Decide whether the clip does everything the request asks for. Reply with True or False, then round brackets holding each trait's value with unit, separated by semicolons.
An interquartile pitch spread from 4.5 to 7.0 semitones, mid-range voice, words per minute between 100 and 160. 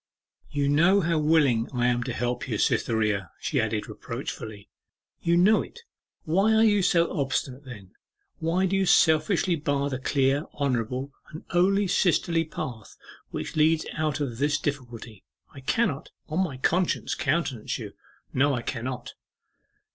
True (5.4 semitones; 145 Hz; 150 wpm)